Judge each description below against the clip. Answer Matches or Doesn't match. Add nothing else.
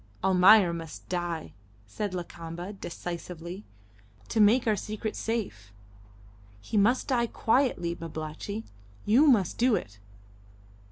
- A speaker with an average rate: Doesn't match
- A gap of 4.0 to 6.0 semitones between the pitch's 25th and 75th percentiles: Matches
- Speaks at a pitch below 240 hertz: Matches